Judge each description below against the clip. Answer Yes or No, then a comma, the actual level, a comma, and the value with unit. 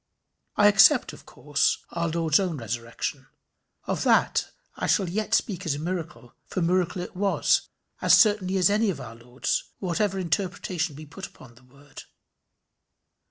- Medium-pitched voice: Yes, medium, 170 Hz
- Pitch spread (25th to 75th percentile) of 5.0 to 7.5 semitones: Yes, average, 5.3 semitones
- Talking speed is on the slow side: No, average, 160 wpm